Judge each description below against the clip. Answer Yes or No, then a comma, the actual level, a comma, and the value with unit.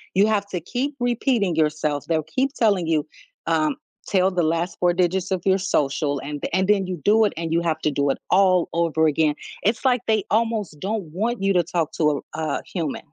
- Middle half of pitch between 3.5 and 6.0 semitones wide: Yes, average, 4.6 semitones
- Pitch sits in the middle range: Yes, medium, 180 Hz